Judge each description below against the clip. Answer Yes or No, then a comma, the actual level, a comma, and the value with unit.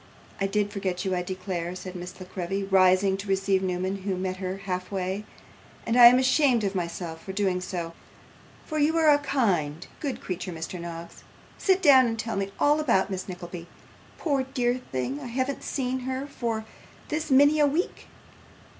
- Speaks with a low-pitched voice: No, high, 195 Hz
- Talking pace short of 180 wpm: No, average, 185 wpm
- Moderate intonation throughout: No, wide, 5.9 semitones